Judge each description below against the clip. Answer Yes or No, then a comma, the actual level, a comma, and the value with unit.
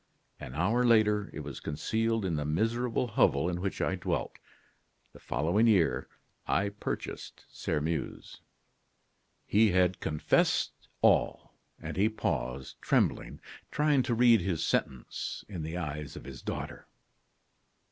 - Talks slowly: Yes, slow, 130 wpm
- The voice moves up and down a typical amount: No, wide, 6.6 semitones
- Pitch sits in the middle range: No, very low, 95 Hz